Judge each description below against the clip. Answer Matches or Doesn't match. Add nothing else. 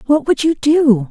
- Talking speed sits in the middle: Doesn't match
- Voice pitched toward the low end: Doesn't match